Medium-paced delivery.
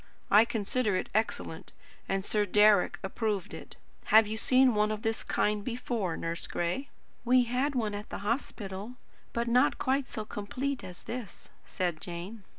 Yes: average, 160 wpm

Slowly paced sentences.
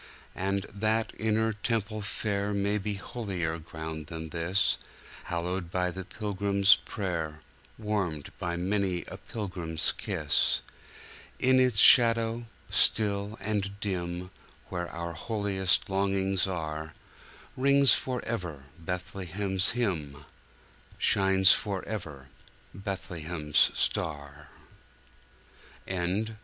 Yes: slow, 85 wpm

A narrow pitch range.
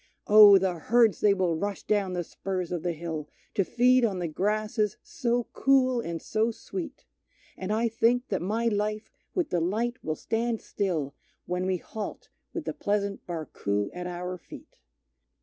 No: average, 4.3 semitones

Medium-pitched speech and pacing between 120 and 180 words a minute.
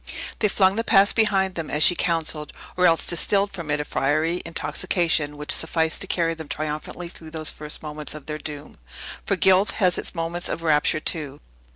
No: medium, 165 Hz; average, 195 wpm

